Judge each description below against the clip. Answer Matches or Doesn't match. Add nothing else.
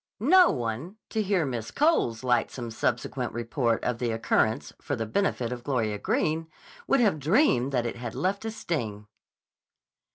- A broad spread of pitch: Matches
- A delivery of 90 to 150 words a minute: Doesn't match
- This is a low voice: Matches